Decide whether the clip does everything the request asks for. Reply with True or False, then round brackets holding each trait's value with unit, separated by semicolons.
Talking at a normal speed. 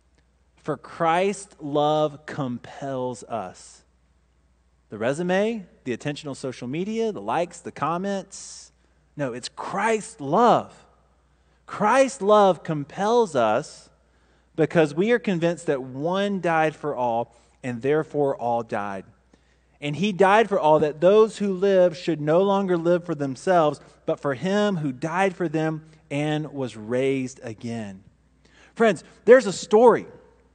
False (130 wpm)